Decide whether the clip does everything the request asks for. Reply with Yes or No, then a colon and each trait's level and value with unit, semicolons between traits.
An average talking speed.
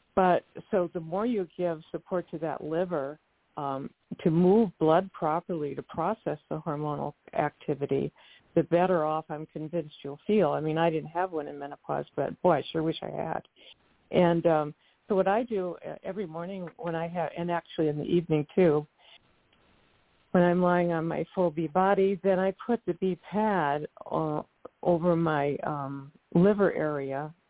Yes: average, 170 wpm